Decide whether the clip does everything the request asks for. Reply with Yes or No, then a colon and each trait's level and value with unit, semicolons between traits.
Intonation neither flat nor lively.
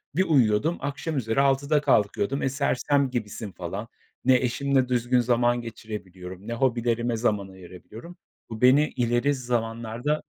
Yes: average, 3.7 semitones